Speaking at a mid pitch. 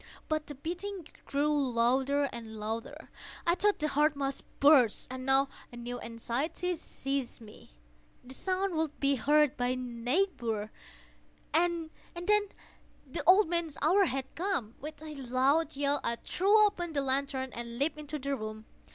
No: very high, 280 Hz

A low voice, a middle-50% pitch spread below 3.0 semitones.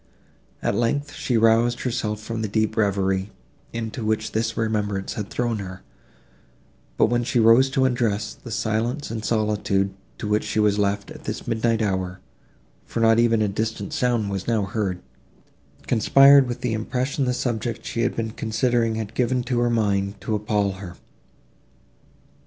Yes: low, 110 Hz; narrow, 2.5 semitones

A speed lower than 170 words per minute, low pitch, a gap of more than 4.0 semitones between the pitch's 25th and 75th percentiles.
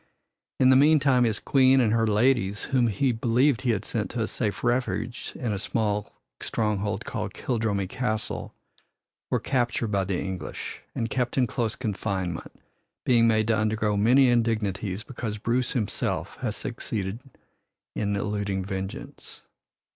No: average, 145 wpm; low, 110 Hz; average, 3.3 semitones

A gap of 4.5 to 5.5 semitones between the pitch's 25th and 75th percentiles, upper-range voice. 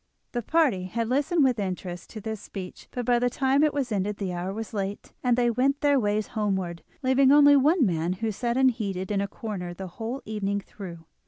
Yes: average, 5.1 semitones; high, 220 Hz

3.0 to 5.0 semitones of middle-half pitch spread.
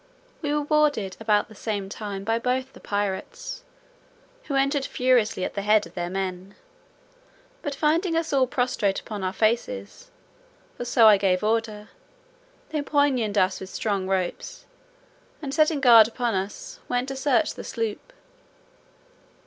No: wide, 5.5 semitones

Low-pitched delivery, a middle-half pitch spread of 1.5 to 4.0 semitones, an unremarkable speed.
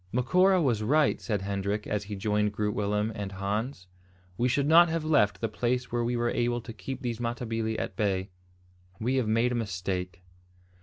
Yes: low, 115 Hz; average, 3.2 semitones; average, 190 wpm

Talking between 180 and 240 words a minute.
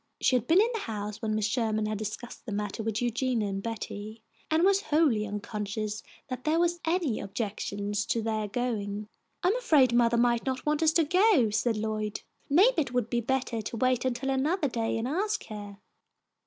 Yes: average, 195 wpm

